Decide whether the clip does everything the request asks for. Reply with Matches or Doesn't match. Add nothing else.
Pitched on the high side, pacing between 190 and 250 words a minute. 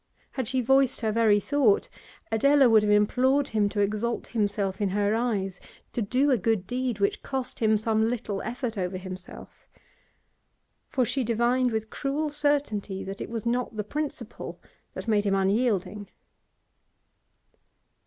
Doesn't match